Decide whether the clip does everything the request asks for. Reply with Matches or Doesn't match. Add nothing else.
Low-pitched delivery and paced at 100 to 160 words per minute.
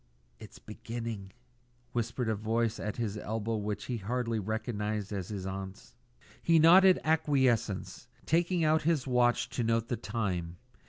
Matches